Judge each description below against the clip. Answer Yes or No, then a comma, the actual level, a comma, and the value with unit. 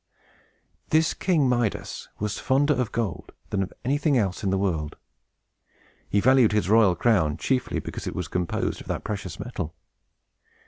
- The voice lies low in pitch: Yes, low, 105 Hz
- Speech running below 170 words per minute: Yes, average, 155 wpm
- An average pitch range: No, wide, 5.7 semitones